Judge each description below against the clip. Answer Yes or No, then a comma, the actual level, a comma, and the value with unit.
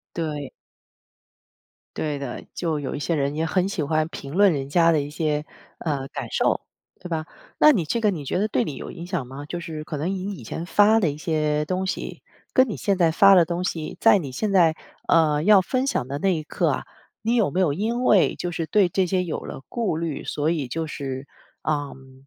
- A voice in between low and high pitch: Yes, medium, 165 Hz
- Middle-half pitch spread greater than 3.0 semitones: Yes, average, 4.2 semitones